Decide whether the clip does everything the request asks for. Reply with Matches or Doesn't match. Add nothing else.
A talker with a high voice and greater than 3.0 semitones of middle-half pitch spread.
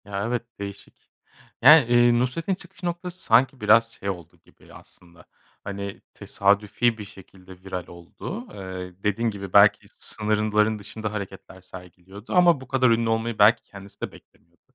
Doesn't match